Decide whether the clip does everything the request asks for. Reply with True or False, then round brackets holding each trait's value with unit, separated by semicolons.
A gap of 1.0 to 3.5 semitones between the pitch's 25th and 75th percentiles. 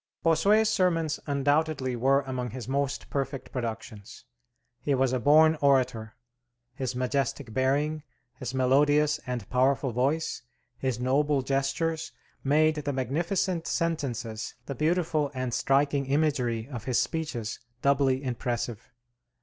True (3.1 semitones)